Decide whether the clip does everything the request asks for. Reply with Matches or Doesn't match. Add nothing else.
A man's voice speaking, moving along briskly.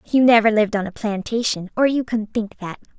Doesn't match